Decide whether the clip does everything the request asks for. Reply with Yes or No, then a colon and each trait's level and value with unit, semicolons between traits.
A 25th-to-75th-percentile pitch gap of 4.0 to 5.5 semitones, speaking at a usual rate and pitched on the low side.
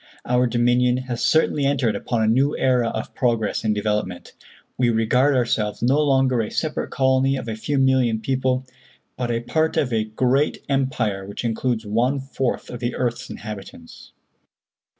No: average, 2.9 semitones; average, 165 wpm; low, 125 Hz